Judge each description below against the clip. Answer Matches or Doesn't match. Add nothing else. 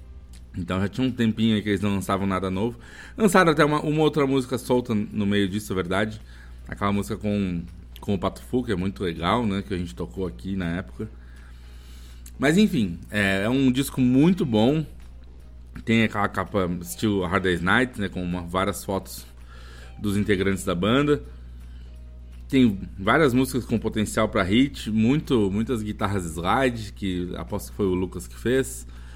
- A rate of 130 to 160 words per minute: Doesn't match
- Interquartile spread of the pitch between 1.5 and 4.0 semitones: Doesn't match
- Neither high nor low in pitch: Doesn't match